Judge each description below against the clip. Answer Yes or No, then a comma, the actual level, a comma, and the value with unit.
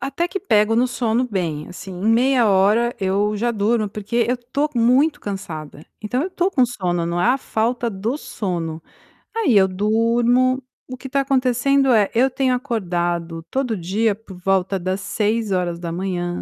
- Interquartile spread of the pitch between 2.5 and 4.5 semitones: No, average, 5.0 semitones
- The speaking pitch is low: No, high, 220 Hz